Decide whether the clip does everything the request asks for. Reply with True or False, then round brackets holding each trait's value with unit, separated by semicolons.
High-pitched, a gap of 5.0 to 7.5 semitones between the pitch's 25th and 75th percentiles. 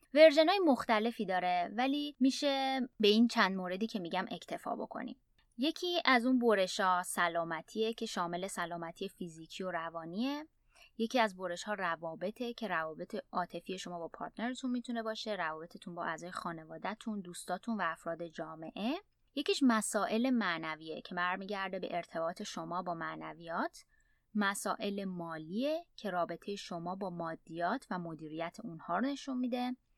True (200 Hz; 5.4 semitones)